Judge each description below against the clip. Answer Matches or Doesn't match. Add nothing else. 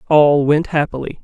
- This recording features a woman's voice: Doesn't match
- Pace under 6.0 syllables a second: Matches